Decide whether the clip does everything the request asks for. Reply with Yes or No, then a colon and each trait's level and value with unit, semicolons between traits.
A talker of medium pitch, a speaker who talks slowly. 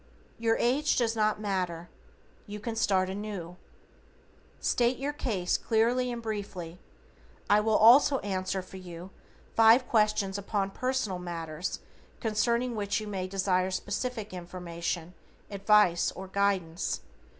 No: high, 200 Hz; slow, 125 wpm